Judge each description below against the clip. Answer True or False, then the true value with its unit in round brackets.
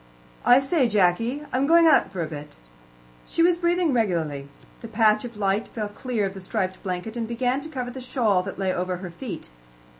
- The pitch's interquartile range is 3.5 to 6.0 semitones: True (5.6 semitones)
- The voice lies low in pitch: False (220 Hz)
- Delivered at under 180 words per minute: False (205 wpm)